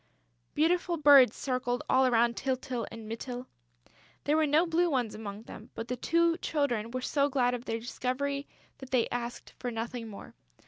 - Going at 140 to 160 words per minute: No, average, 175 wpm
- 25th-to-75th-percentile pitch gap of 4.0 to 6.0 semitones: No, average, 3.3 semitones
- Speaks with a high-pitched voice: Yes, very high, 255 Hz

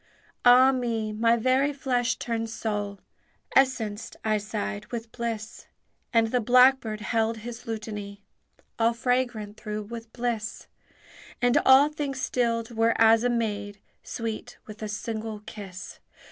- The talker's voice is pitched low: No, high, 225 Hz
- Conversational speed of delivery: No, slow, 130 wpm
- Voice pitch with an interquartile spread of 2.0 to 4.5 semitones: Yes, narrow, 2.4 semitones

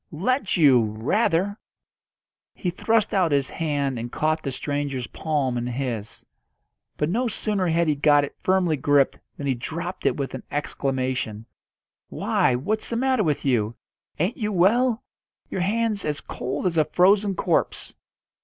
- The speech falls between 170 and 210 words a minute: No, average, 155 wpm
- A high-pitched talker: No, medium, 155 Hz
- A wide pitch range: Yes, wide, 6.6 semitones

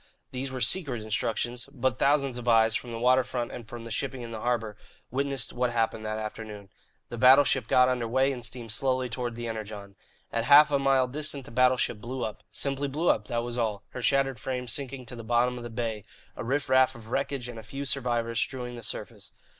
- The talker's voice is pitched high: No, low, 125 Hz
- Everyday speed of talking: No, fast, 220 wpm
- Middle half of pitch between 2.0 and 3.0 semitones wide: Yes, narrow, 2.4 semitones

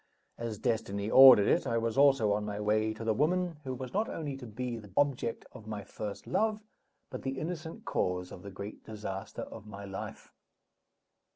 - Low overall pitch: Yes, low, 115 Hz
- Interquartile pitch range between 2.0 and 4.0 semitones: No, average, 4.7 semitones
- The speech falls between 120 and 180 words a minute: No, average, 190 wpm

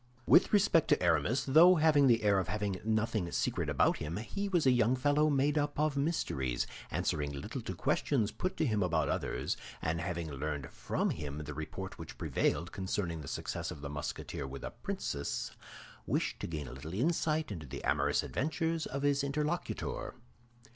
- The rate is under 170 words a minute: No, average, 180 wpm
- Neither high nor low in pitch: No, low, 105 Hz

